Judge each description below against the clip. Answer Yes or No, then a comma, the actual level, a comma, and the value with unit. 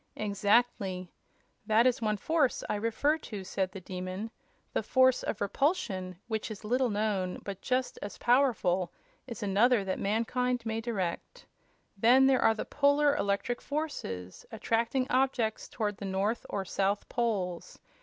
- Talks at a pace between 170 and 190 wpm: No, average, 145 wpm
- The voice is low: No, high, 220 Hz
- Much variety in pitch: No, average, 4.3 semitones